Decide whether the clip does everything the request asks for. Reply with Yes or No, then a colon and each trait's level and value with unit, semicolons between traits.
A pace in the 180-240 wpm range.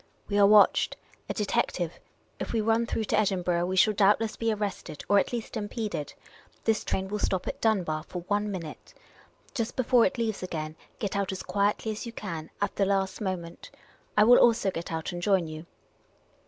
Yes: fast, 205 wpm